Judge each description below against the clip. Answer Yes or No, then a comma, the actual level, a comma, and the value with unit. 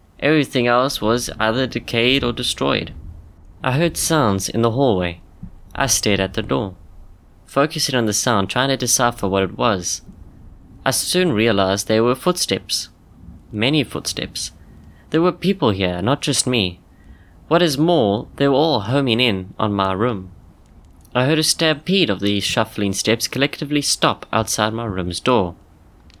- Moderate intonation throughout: No, wide, 6.2 semitones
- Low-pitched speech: Yes, low, 110 Hz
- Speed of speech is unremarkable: Yes, average, 155 wpm